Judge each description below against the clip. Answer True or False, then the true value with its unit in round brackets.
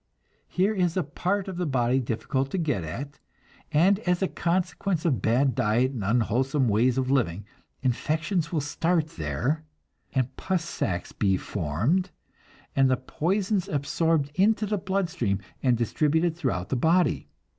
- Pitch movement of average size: False (6.4 semitones)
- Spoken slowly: False (155 wpm)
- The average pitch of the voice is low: False (145 Hz)